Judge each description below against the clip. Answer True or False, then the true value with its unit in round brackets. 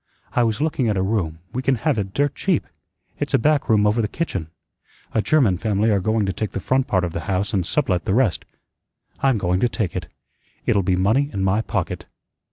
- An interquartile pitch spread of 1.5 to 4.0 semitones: False (5.5 semitones)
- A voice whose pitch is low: True (105 Hz)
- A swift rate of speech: True (225 wpm)